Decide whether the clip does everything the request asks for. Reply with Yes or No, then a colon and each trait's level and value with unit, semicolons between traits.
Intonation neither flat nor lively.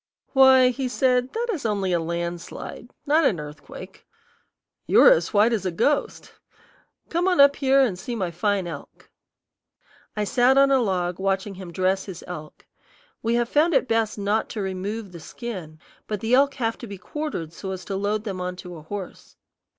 No: wide, 5.8 semitones